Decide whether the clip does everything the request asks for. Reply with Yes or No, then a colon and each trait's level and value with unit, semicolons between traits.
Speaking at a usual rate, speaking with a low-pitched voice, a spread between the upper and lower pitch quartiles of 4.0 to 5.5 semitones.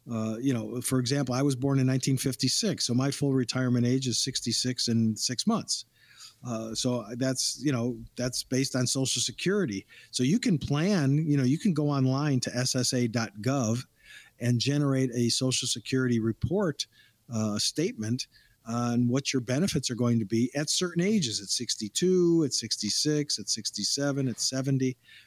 No: average, 165 wpm; low, 130 Hz; average, 2.7 semitones